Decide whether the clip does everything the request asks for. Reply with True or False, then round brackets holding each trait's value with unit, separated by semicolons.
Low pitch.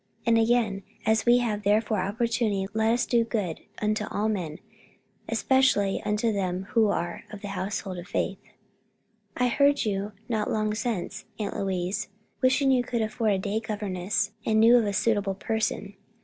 False (215 Hz)